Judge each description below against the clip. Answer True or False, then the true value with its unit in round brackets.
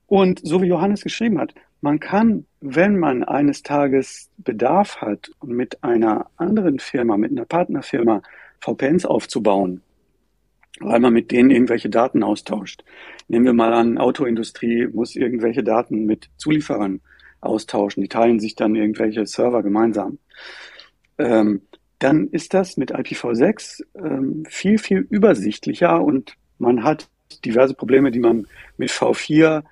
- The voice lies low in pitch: True (125 Hz)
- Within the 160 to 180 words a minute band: False (135 wpm)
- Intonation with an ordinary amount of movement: False (6.2 semitones)